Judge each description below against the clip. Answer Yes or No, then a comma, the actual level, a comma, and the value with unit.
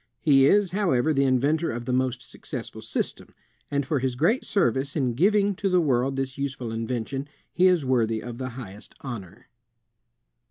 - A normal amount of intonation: Yes, average, 4.4 semitones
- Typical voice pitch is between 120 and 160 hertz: Yes, low, 135 Hz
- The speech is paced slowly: No, average, 170 wpm